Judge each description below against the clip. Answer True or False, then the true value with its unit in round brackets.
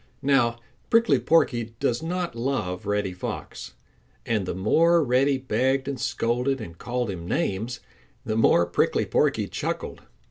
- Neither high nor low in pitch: False (120 Hz)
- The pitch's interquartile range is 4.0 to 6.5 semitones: True (4.7 semitones)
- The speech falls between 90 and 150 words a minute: True (140 wpm)